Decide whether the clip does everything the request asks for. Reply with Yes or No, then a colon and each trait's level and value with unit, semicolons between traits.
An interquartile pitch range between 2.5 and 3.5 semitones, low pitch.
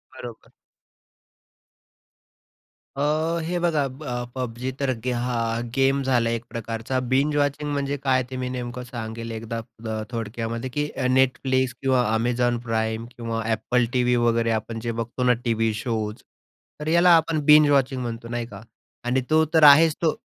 Yes: average, 2.9 semitones; low, 125 Hz